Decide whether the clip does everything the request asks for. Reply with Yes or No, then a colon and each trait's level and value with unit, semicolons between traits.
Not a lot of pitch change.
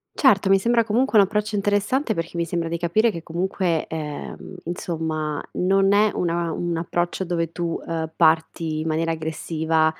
No: average, 3.4 semitones